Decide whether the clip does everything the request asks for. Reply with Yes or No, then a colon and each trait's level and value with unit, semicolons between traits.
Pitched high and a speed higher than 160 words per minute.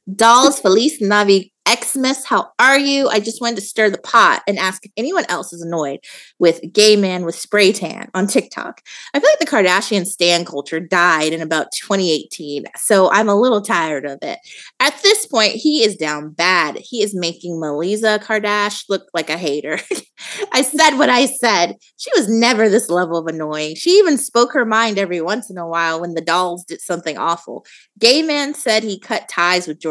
Yes: high, 200 Hz; average, 200 wpm